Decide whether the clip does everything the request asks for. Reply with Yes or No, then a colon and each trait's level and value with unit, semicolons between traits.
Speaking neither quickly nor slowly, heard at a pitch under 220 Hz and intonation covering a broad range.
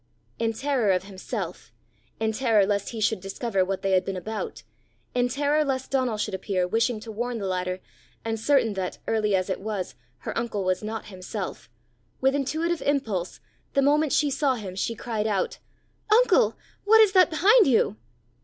No: average, 180 wpm; high, 225 Hz; wide, 5.9 semitones